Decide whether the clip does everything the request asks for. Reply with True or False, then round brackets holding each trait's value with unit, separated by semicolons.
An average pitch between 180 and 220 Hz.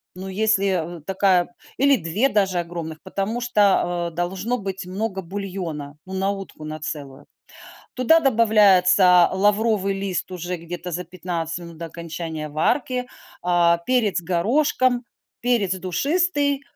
True (190 Hz)